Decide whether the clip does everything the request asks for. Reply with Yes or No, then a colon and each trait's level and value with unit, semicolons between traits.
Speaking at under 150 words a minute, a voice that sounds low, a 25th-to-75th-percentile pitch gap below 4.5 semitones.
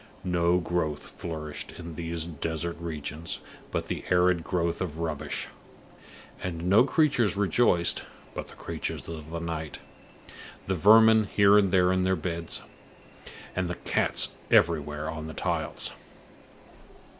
Yes: slow, 135 wpm; very low, 85 Hz; narrow, 2.5 semitones